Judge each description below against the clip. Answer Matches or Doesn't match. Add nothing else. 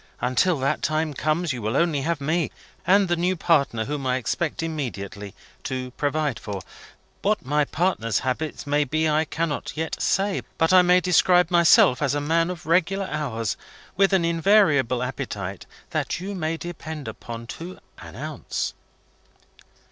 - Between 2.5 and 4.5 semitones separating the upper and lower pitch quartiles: Doesn't match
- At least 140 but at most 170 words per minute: Matches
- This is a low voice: Doesn't match